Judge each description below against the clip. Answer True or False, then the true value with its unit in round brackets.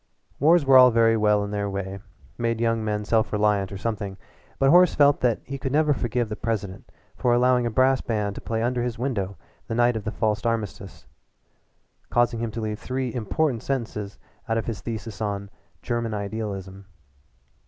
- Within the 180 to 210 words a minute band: True (185 wpm)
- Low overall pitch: True (115 Hz)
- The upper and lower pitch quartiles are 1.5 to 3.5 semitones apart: True (2.9 semitones)